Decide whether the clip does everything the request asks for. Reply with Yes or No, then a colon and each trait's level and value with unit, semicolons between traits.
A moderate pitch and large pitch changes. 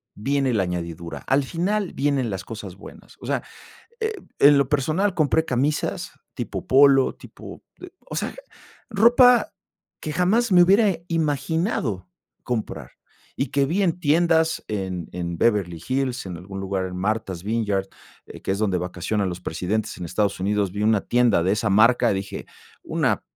No: low, 115 Hz; wide, 8.1 semitones